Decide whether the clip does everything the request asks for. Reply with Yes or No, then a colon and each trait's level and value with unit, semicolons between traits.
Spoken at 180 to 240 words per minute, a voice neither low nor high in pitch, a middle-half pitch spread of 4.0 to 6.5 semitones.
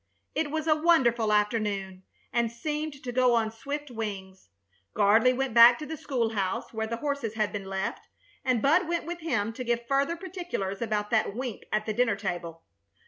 No: average, 190 wpm; high, 235 Hz; average, 5.1 semitones